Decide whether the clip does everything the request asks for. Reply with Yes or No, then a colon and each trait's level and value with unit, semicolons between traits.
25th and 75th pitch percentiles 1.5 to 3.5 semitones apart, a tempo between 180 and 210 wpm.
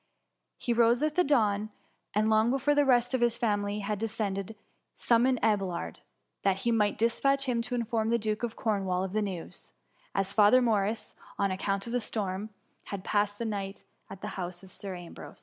Yes: average, 3.1 semitones; average, 190 wpm